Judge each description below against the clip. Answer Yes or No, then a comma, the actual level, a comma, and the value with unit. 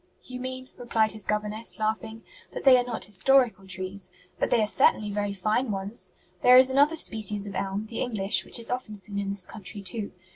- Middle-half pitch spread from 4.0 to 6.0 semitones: No, average, 3.4 semitones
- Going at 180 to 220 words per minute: Yes, fast, 205 wpm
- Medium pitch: No, high, 215 Hz